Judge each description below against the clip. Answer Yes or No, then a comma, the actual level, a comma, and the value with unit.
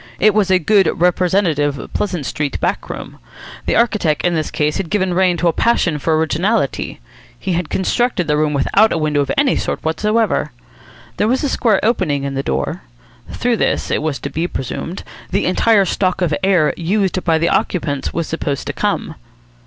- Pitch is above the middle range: No, medium, 175 Hz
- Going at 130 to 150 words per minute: No, average, 190 wpm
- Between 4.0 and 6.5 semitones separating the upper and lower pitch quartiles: Yes, average, 4.8 semitones